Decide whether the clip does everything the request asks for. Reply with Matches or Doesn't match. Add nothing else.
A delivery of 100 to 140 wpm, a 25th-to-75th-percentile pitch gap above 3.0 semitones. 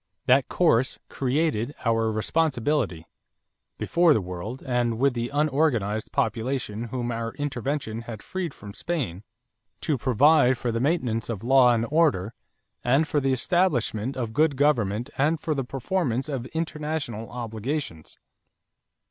Matches